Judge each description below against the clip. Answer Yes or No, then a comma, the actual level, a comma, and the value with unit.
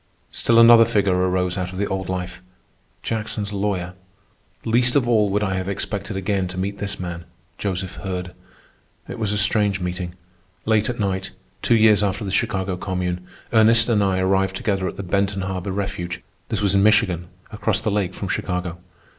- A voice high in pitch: No, low, 100 Hz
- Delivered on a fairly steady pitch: Yes, narrow, 2.3 semitones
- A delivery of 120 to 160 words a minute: No, average, 180 wpm